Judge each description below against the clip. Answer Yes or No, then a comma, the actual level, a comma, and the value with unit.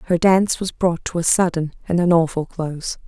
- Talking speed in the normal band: No, fast, 215 wpm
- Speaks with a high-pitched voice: No, medium, 170 Hz